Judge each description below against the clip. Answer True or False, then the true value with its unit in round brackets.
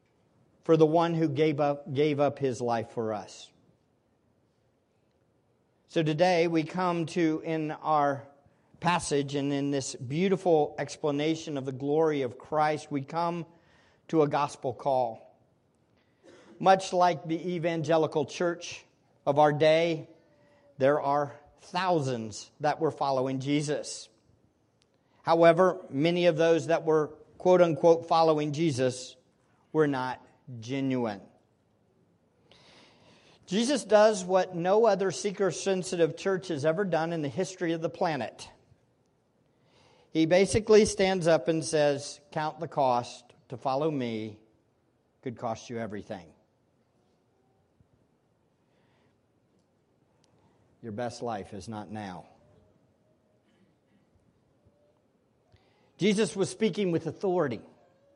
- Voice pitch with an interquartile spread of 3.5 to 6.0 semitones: True (4.2 semitones)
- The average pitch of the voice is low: False (155 Hz)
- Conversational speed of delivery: False (110 wpm)